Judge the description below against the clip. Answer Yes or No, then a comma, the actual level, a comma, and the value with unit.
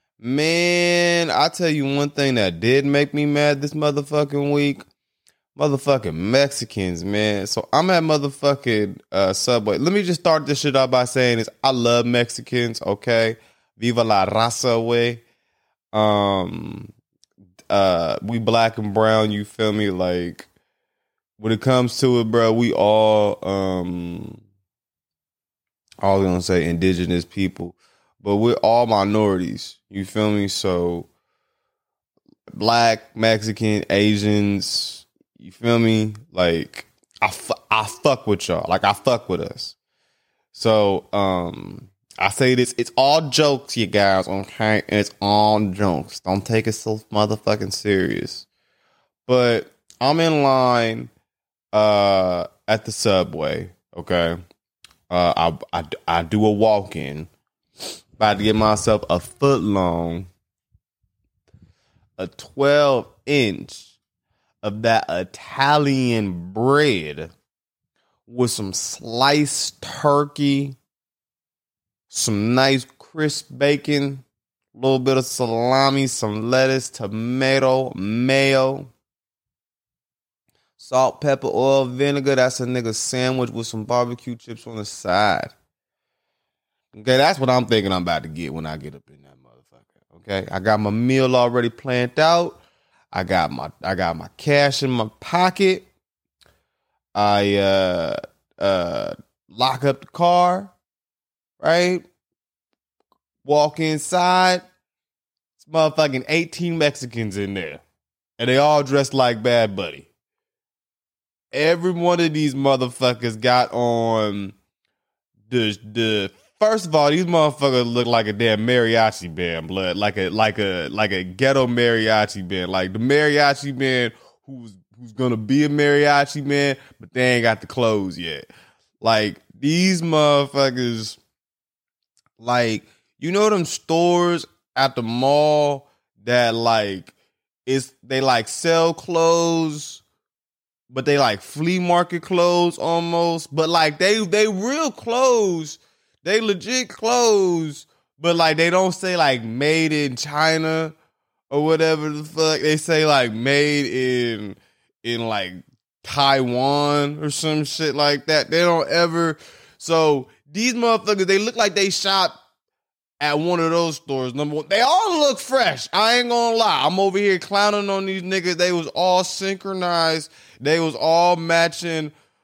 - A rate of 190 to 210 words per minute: No, slow, 135 wpm